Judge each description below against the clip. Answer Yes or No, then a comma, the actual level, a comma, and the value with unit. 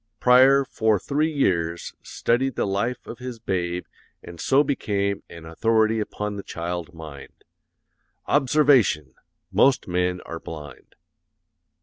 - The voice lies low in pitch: Yes, low, 105 Hz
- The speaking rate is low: Yes, slow, 120 wpm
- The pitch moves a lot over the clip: Yes, wide, 6.6 semitones